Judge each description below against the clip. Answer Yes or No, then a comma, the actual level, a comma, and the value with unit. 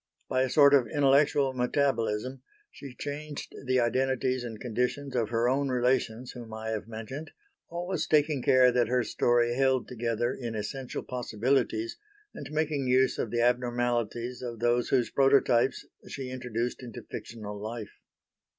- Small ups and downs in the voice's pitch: Yes, narrow, 2.3 semitones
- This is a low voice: Yes, low, 125 Hz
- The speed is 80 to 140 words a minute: No, average, 150 wpm